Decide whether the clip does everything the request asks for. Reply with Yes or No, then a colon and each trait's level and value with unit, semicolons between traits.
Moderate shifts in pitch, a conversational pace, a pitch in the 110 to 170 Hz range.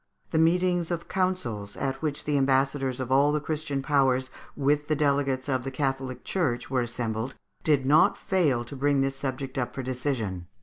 No: narrow, 2.2 semitones; average, 180 wpm; low, 135 Hz